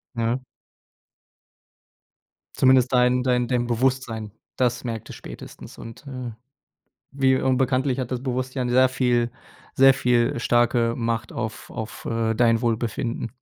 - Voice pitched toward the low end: Yes, low, 125 Hz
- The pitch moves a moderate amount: No, narrow, 1.8 semitones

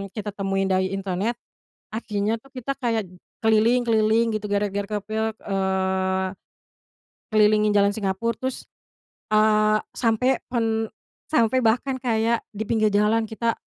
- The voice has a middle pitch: No, high, 215 Hz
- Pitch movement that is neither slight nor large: No, narrow, 2.2 semitones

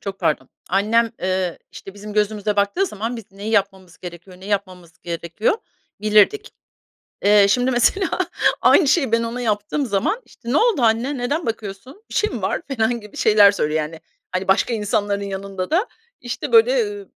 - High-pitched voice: Yes, high, 210 Hz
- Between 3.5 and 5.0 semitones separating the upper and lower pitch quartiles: Yes, average, 4.2 semitones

